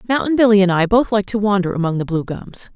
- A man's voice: No, female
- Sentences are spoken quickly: Yes, fast, 260 wpm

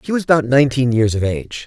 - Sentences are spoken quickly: Yes, fast, 255 wpm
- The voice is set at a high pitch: No, low, 130 Hz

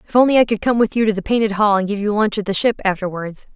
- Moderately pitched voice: No, high, 210 Hz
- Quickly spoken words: Yes, fast, 320 wpm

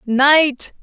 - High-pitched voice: Yes, very high, 275 Hz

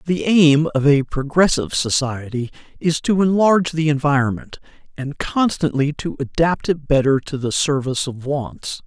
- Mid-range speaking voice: Yes, medium, 145 Hz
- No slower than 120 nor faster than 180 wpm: Yes, average, 150 wpm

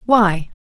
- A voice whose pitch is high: Yes, high, 200 Hz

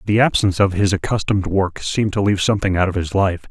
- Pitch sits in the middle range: No, low, 100 Hz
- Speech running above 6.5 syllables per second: Yes, 6.9 syllables/s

